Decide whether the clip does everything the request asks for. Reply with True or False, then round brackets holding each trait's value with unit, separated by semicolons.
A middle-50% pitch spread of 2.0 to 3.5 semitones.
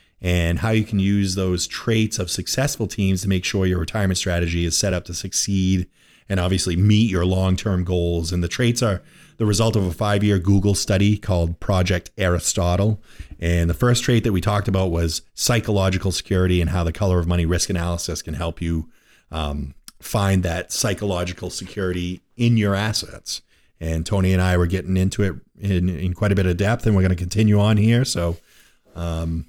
True (2.8 semitones)